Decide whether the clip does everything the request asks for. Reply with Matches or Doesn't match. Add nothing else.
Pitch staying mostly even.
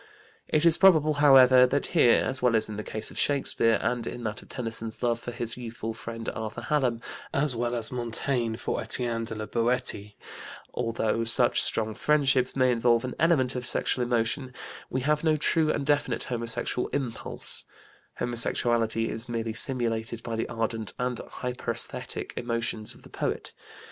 Matches